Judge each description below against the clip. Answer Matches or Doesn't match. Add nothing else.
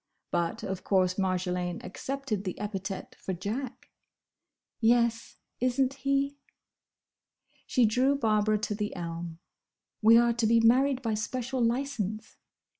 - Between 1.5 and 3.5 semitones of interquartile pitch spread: Doesn't match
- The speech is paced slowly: Matches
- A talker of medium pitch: Doesn't match